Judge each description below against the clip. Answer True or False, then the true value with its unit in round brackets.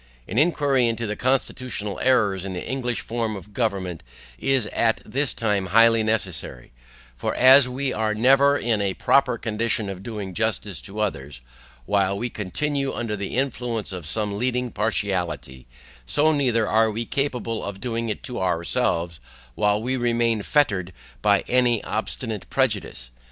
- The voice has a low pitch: True (110 Hz)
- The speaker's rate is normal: True (155 wpm)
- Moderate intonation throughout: True (3.9 semitones)